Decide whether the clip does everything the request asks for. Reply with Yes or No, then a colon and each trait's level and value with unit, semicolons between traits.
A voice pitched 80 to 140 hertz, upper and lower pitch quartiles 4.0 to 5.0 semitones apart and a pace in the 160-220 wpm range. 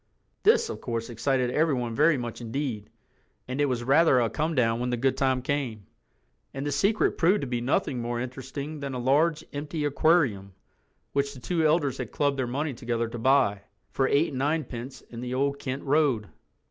No: low, 135 Hz; average, 3.3 semitones; average, 185 wpm